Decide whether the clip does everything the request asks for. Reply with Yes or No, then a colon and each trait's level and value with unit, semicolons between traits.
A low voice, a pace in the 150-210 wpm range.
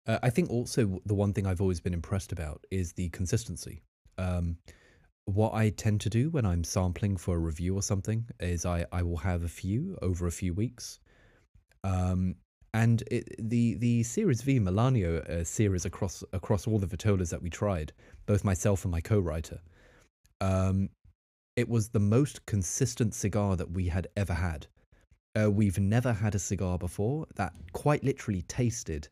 Yes: low, 100 Hz; average, 175 wpm